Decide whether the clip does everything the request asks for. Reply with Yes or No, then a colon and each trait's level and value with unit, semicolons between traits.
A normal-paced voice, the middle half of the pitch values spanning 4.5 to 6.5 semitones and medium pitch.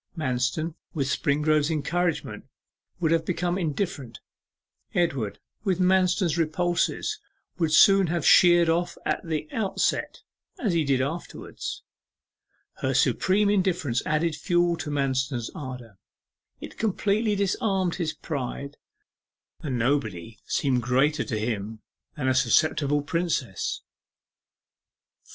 No: slow, 115 wpm; average, 5.1 semitones; medium, 155 Hz